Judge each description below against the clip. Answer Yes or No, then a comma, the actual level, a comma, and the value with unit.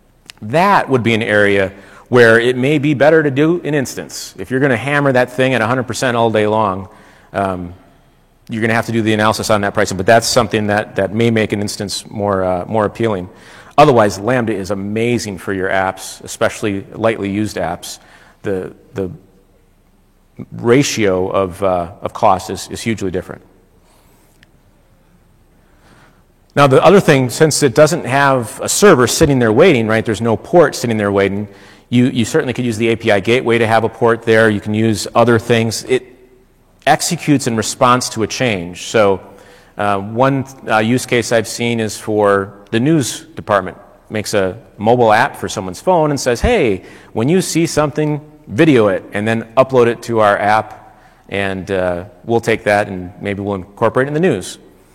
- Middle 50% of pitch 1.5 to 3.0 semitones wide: No, average, 4.0 semitones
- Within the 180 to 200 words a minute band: Yes, average, 185 wpm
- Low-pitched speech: Yes, low, 110 Hz